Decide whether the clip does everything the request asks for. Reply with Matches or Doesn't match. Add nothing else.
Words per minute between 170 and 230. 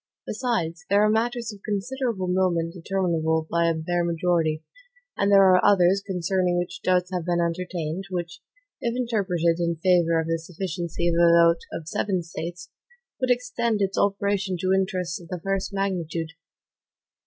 Doesn't match